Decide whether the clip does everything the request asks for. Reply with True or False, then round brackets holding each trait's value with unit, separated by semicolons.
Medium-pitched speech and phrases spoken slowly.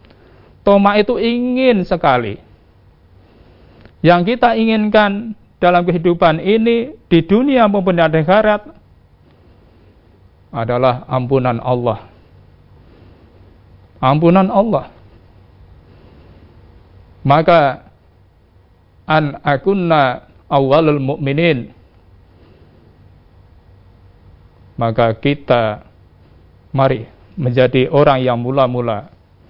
False (115 Hz; 65 wpm)